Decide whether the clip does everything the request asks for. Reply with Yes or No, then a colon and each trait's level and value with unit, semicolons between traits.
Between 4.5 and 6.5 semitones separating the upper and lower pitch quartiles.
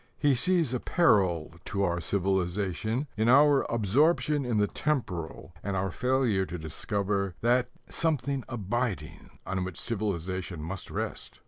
Yes: wide, 5.5 semitones